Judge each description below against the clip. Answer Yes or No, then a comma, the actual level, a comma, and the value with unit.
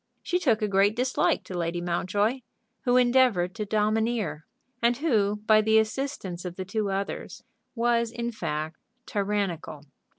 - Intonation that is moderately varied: Yes, average, 4.1 semitones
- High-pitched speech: Yes, high, 215 Hz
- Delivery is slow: No, average, 145 wpm